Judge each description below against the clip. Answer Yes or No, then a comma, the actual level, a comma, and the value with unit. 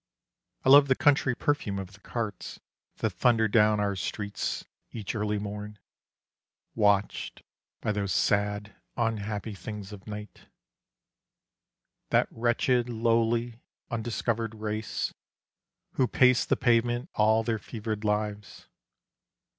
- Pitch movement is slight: Yes, narrow, 2.2 semitones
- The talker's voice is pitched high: No, low, 110 Hz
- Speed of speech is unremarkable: No, slow, 115 wpm